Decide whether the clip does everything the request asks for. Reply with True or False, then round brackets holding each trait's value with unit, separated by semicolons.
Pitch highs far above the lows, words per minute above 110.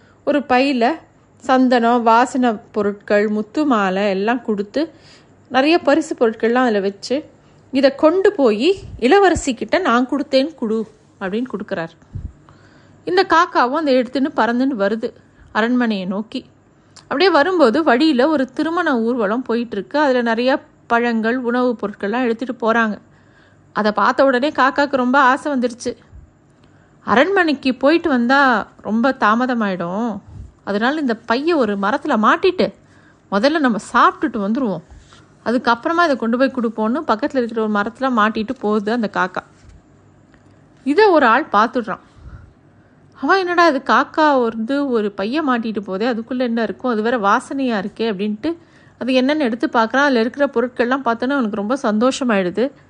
False (4.1 semitones; 130 wpm)